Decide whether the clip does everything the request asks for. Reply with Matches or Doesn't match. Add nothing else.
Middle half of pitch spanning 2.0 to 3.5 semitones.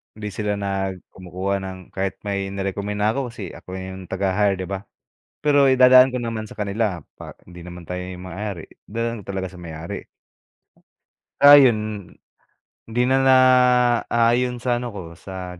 Doesn't match